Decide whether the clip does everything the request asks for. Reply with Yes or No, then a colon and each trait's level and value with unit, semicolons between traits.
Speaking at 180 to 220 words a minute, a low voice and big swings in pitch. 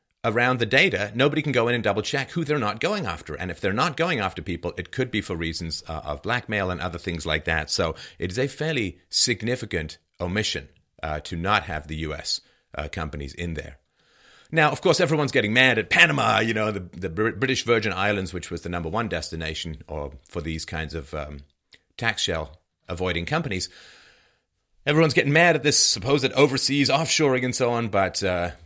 Yes: average, 200 wpm; very low, 95 Hz; wide, 7.5 semitones